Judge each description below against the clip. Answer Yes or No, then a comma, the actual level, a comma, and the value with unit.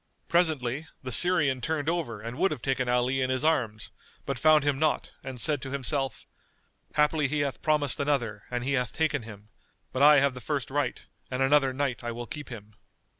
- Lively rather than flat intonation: No, average, 3.3 semitones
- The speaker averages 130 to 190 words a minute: No, average, 200 wpm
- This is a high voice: No, low, 135 Hz